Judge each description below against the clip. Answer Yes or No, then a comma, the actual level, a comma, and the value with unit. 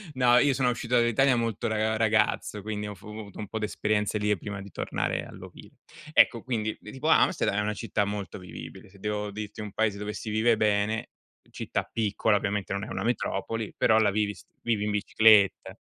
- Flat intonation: Yes, narrow, 1.6 semitones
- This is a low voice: Yes, low, 105 Hz